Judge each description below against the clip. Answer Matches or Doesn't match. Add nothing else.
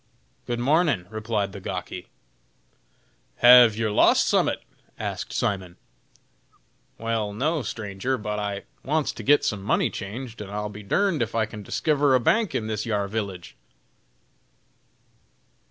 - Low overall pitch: Matches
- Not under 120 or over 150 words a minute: Matches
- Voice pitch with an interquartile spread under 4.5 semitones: Matches